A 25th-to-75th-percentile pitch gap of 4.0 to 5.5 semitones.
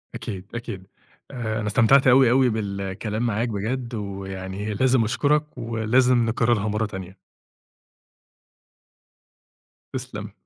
No: average, 3.3 semitones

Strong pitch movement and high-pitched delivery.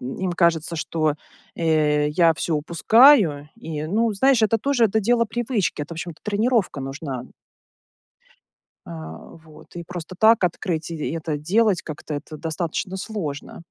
No: wide, 5.9 semitones; medium, 170 Hz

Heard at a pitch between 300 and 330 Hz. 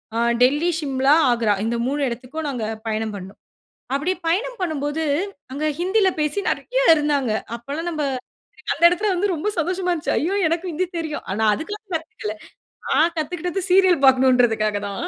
Yes: very high, 310 Hz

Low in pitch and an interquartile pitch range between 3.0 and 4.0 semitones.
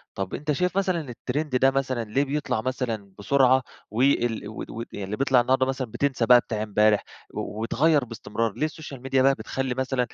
Yes: low, 130 Hz; average, 3.3 semitones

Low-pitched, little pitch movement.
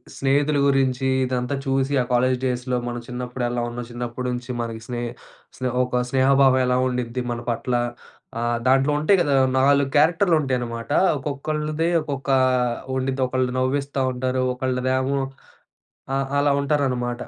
Yes: low, 130 Hz; narrow, 2.0 semitones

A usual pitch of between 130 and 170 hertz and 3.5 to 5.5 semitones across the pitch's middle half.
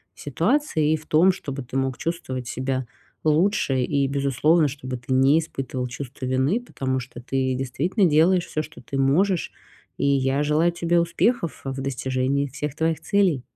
Yes: medium, 140 Hz; average, 3.8 semitones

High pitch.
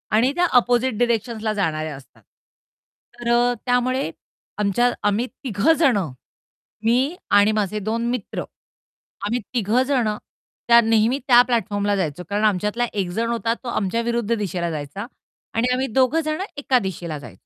Yes: high, 230 Hz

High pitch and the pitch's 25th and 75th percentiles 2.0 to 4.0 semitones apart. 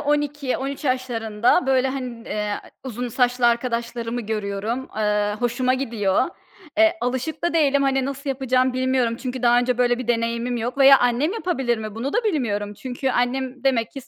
Yes: very high, 250 Hz; narrow, 2.4 semitones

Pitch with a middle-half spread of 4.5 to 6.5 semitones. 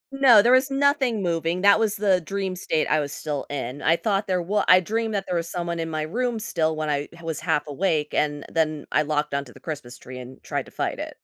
Yes: average, 5.2 semitones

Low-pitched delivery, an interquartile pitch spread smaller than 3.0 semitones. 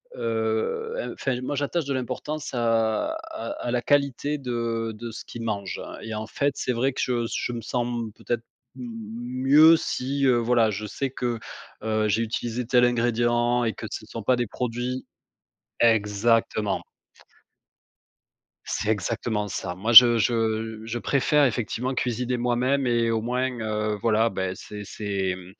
Yes: low, 120 Hz; narrow, 2.4 semitones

